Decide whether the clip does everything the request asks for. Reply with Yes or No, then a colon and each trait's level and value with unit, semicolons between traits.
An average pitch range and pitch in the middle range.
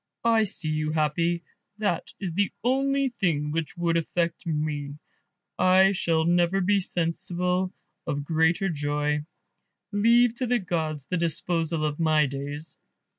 Yes: average, 3.7 semitones; medium, 170 Hz